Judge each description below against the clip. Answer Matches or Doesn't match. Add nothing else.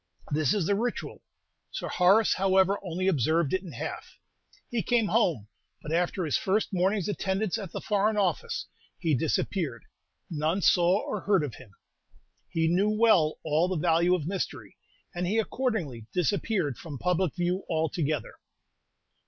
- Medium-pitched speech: Matches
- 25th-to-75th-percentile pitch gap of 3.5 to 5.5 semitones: Matches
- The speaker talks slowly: Doesn't match